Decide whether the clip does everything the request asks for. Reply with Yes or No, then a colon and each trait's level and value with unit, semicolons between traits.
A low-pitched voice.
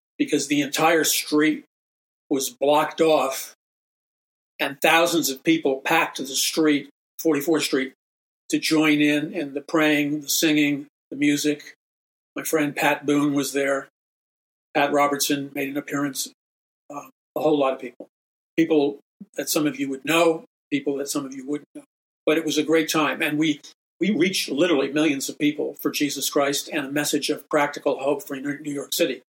No: medium, 145 Hz